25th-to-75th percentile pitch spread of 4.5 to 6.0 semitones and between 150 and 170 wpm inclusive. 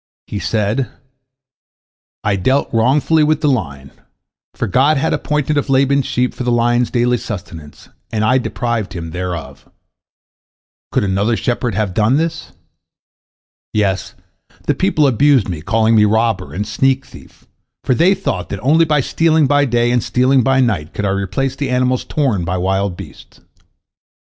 Yes: average, 5.2 semitones; average, 160 wpm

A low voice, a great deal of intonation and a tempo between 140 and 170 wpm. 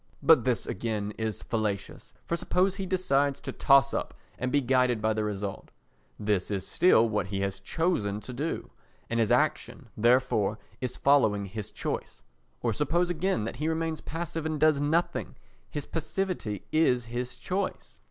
Yes: low, 125 Hz; wide, 6.9 semitones; average, 160 wpm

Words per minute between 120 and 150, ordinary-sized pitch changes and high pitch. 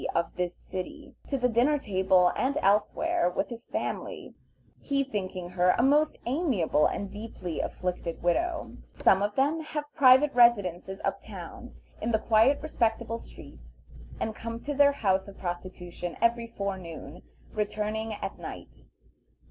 No: average, 145 wpm; wide, 6.5 semitones; high, 220 Hz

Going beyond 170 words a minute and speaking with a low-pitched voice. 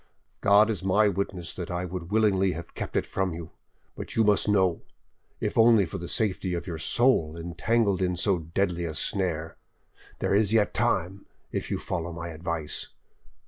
Yes: average, 180 wpm; very low, 90 Hz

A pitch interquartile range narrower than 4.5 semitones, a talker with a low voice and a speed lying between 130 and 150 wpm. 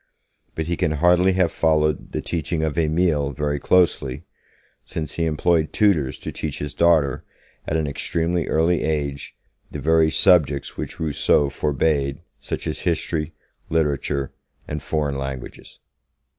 Yes: narrow, 2.5 semitones; very low, 75 Hz; average, 140 wpm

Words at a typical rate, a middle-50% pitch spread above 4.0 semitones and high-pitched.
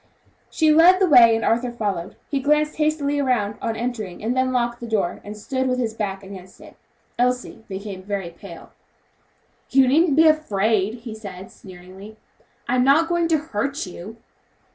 Yes: average, 170 wpm; wide, 5.6 semitones; high, 235 Hz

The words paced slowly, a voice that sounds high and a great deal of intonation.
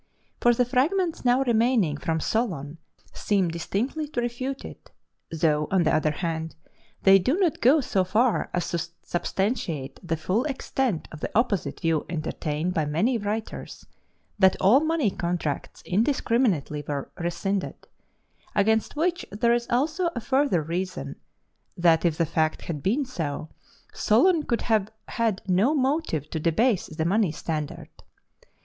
No: average, 145 wpm; high, 195 Hz; wide, 7.3 semitones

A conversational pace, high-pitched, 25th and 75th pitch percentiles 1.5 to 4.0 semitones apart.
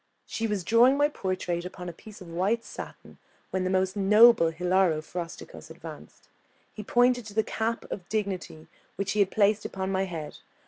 Yes: average, 180 wpm; high, 195 Hz; average, 3.4 semitones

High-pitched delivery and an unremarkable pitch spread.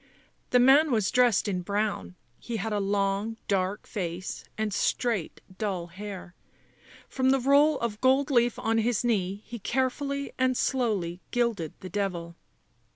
Yes: high, 215 Hz; average, 4.4 semitones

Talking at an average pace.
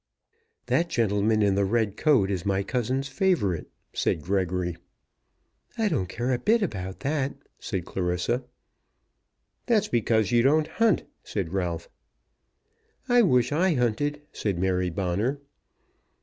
No: slow, 130 wpm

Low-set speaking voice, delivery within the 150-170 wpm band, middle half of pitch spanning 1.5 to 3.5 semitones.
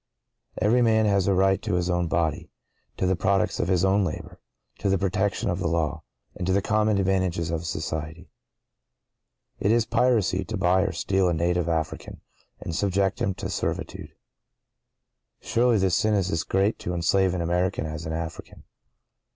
Yes: very low, 95 Hz; average, 165 wpm; narrow, 2.6 semitones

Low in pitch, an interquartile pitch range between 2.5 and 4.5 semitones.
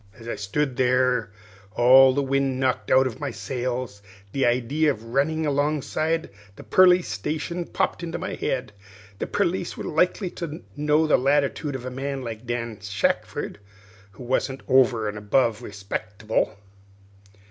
Yes: low, 130 Hz; average, 4.1 semitones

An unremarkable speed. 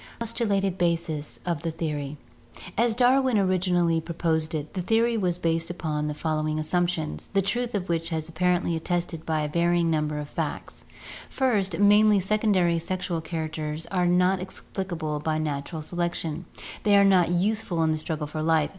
Yes: average, 170 wpm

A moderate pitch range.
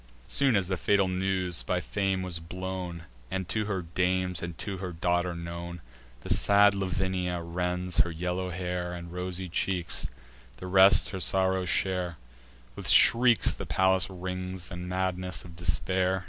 No: narrow, 1.2 semitones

